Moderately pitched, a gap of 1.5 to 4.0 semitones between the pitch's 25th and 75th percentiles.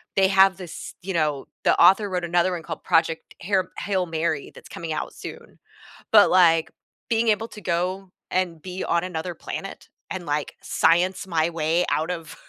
Yes: medium, 175 Hz; narrow, 2.5 semitones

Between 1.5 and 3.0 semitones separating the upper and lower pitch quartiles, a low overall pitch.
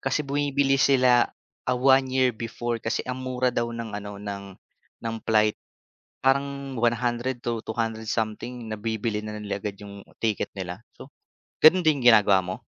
No: average, 3.5 semitones; low, 120 Hz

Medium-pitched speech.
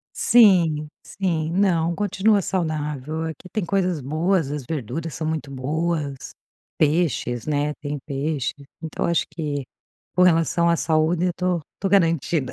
Yes: medium, 160 Hz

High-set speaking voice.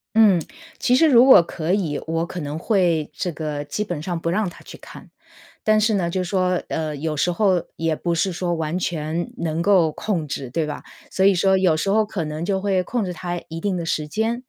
No: medium, 175 Hz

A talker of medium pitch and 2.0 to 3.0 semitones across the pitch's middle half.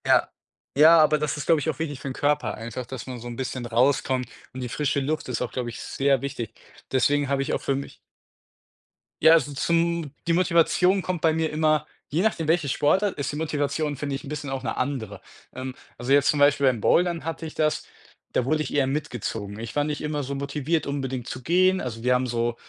No: medium, 145 Hz; average, 3.4 semitones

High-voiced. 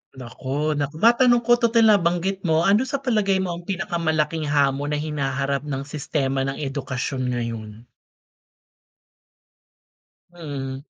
No: medium, 150 Hz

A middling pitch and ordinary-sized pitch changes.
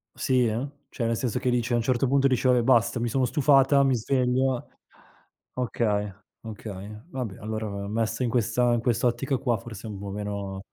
No: low, 120 Hz; average, 3.0 semitones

